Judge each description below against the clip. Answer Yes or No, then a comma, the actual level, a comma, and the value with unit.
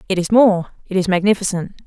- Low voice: No, high, 195 Hz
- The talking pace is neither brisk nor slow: Yes, average, 160 wpm